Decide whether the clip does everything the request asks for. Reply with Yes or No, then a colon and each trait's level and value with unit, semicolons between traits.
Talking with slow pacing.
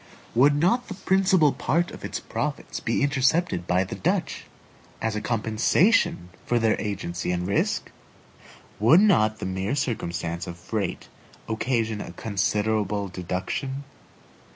Yes: slow, 130 wpm